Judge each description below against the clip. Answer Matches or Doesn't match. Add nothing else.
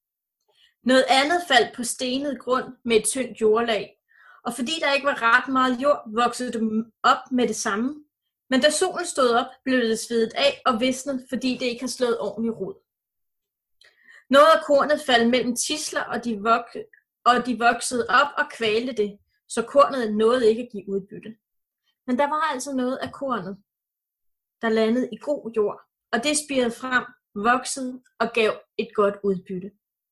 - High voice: Matches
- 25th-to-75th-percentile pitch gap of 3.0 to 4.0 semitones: Matches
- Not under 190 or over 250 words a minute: Doesn't match